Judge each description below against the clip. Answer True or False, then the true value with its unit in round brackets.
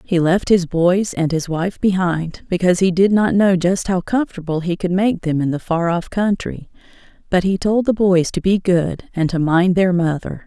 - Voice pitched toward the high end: False (180 Hz)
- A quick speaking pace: True (220 wpm)